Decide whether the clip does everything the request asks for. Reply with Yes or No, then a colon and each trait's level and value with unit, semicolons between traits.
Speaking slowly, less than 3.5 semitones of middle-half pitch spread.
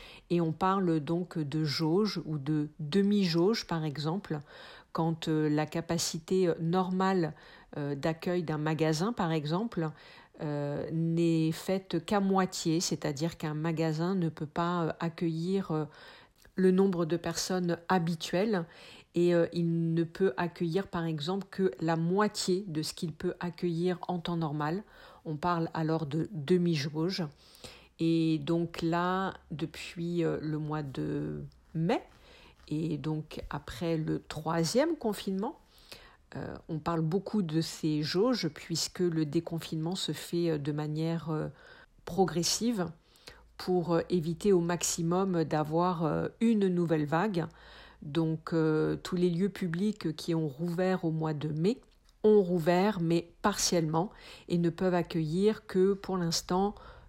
Yes: slow, 125 wpm; narrow, 2.4 semitones